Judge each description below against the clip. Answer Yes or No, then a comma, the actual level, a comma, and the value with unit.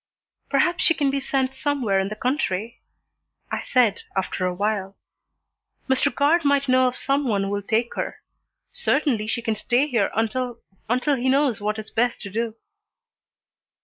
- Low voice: No, high, 240 Hz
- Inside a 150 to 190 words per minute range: Yes, average, 170 wpm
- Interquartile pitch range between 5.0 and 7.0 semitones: No, average, 4.3 semitones